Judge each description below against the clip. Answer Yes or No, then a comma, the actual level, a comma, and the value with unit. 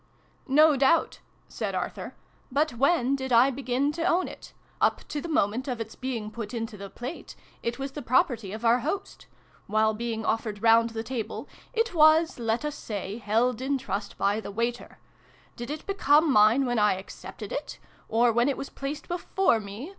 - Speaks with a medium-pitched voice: No, high, 245 Hz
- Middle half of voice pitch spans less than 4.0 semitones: No, average, 4.3 semitones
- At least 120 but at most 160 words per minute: No, average, 190 wpm